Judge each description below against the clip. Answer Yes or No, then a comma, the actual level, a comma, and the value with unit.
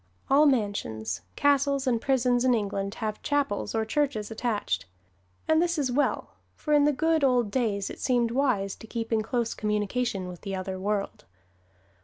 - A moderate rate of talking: Yes, average, 170 wpm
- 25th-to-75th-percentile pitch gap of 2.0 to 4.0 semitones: No, average, 5.0 semitones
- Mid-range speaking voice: No, high, 235 Hz